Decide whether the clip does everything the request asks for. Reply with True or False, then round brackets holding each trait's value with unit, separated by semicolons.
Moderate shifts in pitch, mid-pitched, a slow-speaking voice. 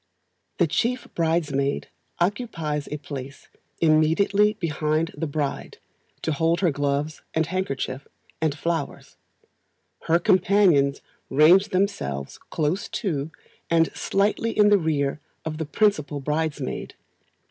True (4.3 semitones; 160 Hz; 115 wpm)